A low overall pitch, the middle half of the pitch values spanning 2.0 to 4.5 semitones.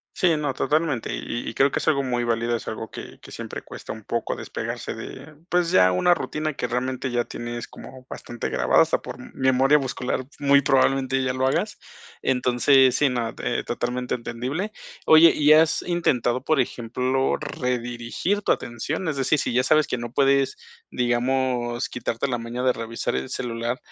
Yes: low, 130 Hz; average, 2.8 semitones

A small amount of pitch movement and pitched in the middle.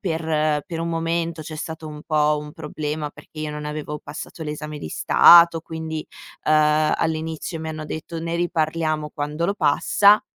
Yes: narrow, 1.4 semitones; medium, 155 Hz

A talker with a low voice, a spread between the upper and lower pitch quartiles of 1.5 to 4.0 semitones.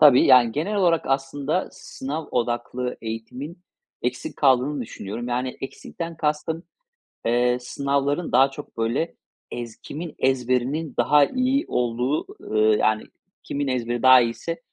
Yes: low, 130 Hz; average, 3.6 semitones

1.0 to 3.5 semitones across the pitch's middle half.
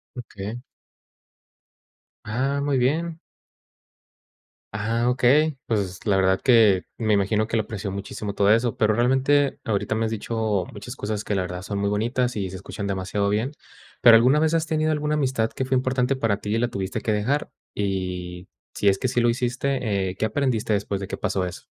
No: average, 4.2 semitones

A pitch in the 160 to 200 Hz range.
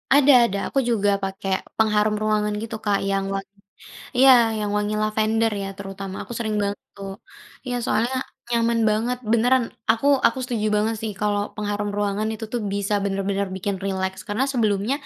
No: high, 210 Hz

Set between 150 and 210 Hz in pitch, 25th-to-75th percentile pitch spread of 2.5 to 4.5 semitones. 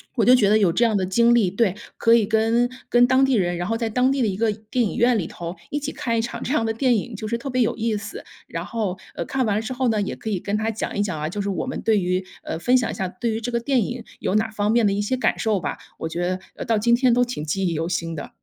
No: high, 220 Hz; average, 3.5 semitones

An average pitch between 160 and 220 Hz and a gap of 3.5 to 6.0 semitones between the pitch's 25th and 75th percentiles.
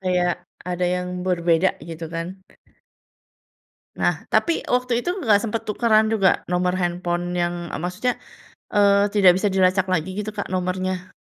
No: medium, 185 Hz; narrow, 2.6 semitones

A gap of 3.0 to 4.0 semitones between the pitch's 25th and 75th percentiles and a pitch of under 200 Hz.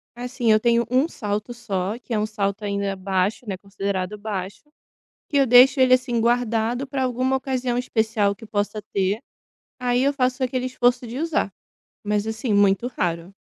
No: average, 3.7 semitones; high, 230 Hz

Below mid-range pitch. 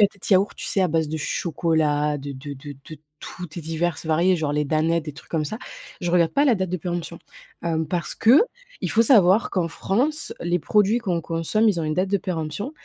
No: medium, 170 Hz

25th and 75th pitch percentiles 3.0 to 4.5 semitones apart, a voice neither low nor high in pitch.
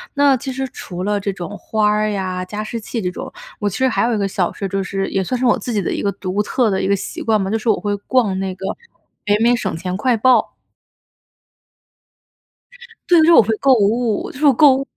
No: average, 4.0 semitones; high, 210 Hz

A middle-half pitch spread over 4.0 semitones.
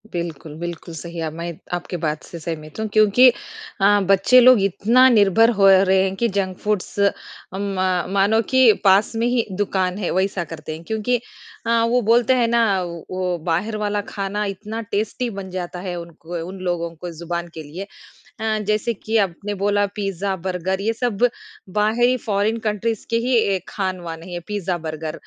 No: average, 3.7 semitones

